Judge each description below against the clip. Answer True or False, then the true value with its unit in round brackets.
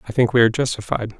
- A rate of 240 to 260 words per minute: True (250 wpm)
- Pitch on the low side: True (115 Hz)